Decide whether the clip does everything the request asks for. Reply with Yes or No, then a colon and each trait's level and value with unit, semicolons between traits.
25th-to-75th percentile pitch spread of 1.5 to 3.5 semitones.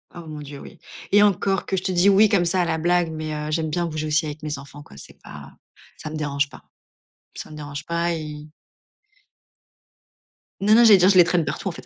Yes: average, 3.0 semitones